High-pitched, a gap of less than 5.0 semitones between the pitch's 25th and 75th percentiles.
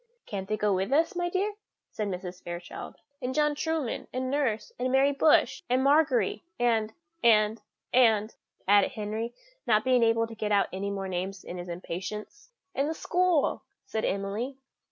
No: high, 225 Hz; average, 5.3 semitones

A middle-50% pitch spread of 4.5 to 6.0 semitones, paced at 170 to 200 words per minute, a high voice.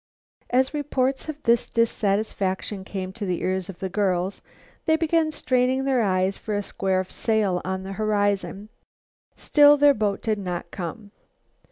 No: average, 5.2 semitones; average, 155 wpm; high, 205 Hz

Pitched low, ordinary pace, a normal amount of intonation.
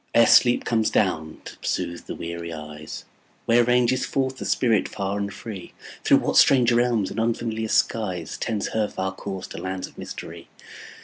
Yes: low, 110 Hz; average, 175 wpm; average, 4.1 semitones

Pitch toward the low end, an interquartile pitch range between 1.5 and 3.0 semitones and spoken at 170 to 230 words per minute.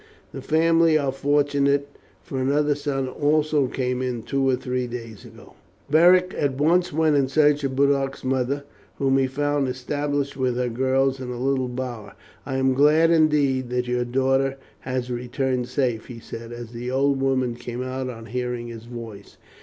Yes: low, 130 Hz; narrow, 2.4 semitones; average, 175 wpm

